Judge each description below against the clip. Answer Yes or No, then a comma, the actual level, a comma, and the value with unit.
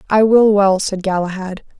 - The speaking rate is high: No, average, 165 wpm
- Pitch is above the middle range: Yes, high, 200 Hz